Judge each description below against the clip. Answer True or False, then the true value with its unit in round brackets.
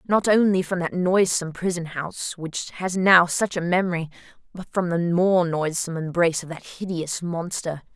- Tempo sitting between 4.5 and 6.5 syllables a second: True (5.0 syllables/s)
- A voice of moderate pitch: True (175 Hz)